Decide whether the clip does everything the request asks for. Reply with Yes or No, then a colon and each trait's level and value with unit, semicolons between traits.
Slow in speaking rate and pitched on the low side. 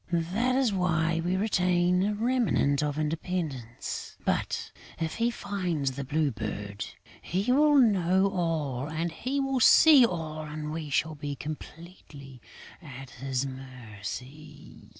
No: slow, 130 wpm; medium, 160 Hz